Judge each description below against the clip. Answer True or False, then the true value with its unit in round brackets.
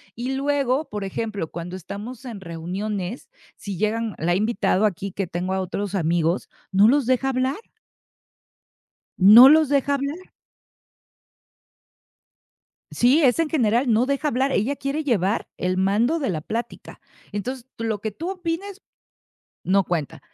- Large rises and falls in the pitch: True (5.9 semitones)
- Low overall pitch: False (225 Hz)